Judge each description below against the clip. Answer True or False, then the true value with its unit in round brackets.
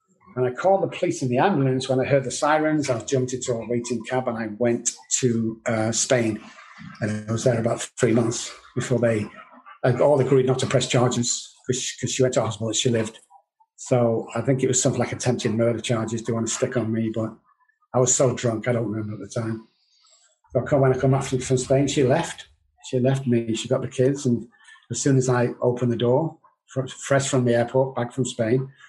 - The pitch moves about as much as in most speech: False (2.2 semitones)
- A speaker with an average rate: False (220 wpm)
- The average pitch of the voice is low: True (125 Hz)